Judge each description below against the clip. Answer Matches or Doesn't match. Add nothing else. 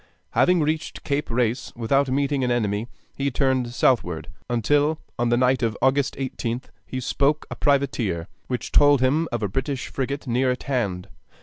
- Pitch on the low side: Matches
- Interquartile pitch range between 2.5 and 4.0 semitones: Matches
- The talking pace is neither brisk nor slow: Matches